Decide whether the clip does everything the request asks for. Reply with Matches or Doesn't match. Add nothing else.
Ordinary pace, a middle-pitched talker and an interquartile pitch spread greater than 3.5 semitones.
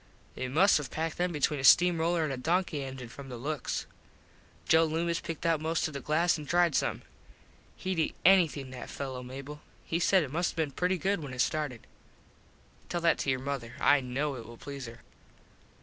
Doesn't match